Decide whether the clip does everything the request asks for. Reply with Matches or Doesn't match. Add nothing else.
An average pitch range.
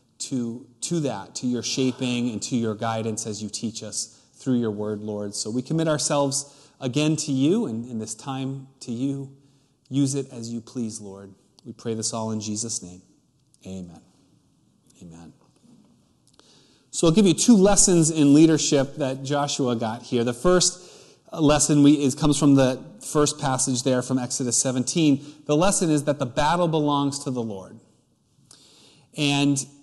Matches